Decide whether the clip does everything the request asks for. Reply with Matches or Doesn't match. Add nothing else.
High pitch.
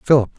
Doesn't match